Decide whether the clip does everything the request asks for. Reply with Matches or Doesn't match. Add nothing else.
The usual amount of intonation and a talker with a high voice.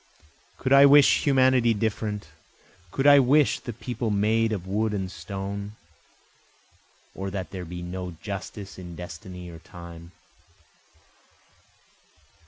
Doesn't match